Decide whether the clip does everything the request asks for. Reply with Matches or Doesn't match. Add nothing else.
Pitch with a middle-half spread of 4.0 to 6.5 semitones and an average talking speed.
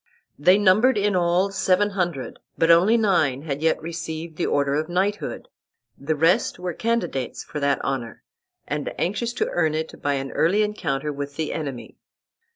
Matches